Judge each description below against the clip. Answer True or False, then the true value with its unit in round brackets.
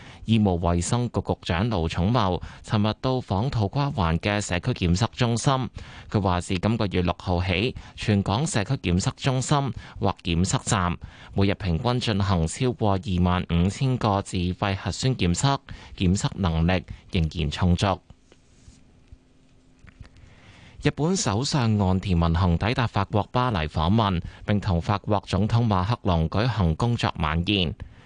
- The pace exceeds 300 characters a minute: False (220 characters per minute)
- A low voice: True (100 Hz)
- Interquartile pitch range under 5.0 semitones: True (4.6 semitones)